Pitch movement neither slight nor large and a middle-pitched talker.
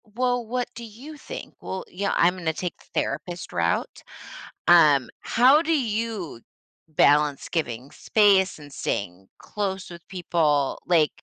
No: wide, 7.1 semitones; medium, 180 Hz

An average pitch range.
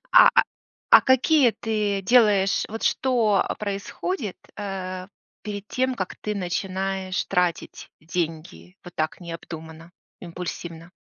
Yes: average, 3.2 semitones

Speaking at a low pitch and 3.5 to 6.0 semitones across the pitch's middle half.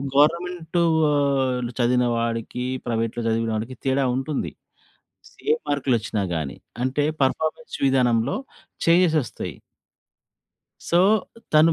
Yes: low, 130 Hz; average, 4.5 semitones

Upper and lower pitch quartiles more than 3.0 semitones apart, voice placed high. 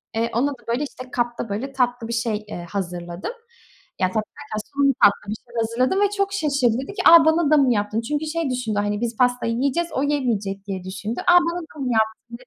Yes: average, 5.1 semitones; high, 240 Hz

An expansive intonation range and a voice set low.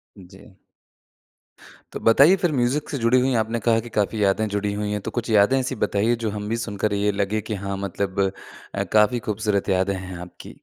No: average, 2.7 semitones; low, 105 Hz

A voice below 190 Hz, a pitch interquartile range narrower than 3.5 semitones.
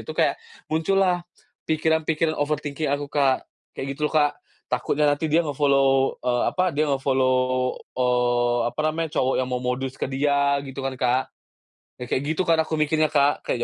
Yes: medium, 140 Hz; average, 2.9 semitones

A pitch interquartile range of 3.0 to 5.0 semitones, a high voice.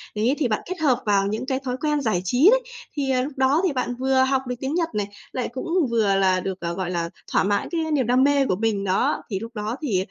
No: wide, 5.5 semitones; very high, 250 Hz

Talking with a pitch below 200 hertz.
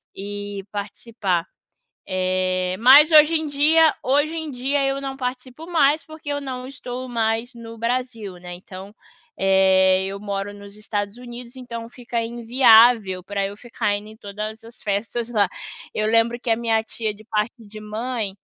No: high, 230 Hz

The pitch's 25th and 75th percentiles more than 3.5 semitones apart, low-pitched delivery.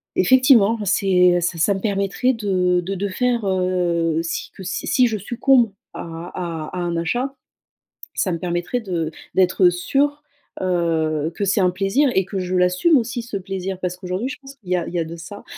No: average, 4.1 semitones; medium, 185 Hz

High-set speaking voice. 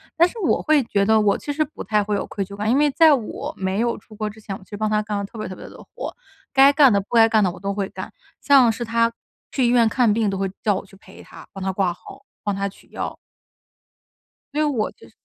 Yes: high, 215 Hz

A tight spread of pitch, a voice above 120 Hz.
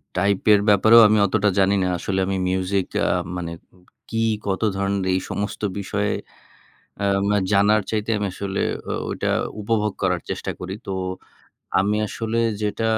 No: narrow, 1.7 semitones; low, 100 Hz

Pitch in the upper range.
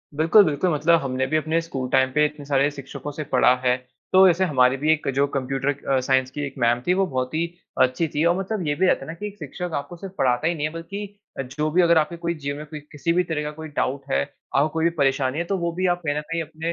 No: medium, 150 Hz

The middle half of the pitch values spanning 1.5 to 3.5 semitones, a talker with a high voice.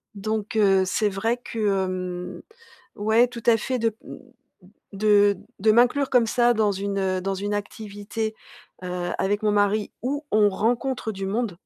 Yes: narrow, 2.6 semitones; high, 210 Hz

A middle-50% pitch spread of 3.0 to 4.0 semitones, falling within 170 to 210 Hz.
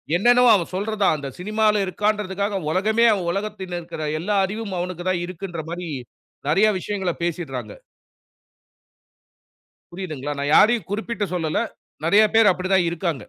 Yes: average, 3.5 semitones; high, 190 Hz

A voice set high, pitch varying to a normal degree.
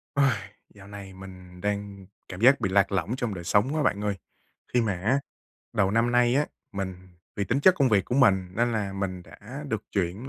No: low, 105 Hz; average, 4.2 semitones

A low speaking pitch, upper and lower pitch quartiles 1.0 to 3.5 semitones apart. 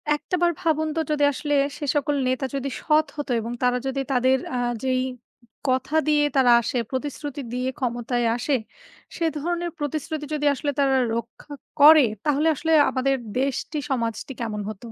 No: very high, 275 Hz; average, 2.9 semitones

